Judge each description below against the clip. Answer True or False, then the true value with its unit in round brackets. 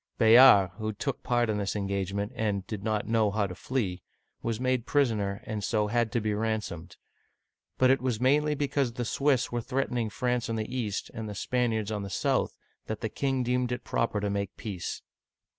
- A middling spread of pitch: True (3.4 semitones)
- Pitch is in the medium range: False (110 Hz)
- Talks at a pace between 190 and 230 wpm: True (195 wpm)